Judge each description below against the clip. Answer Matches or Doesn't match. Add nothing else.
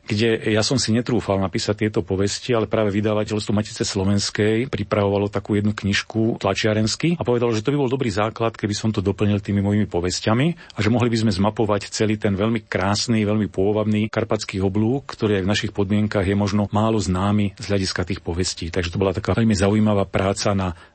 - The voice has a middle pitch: Doesn't match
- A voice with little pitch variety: Matches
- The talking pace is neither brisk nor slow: Doesn't match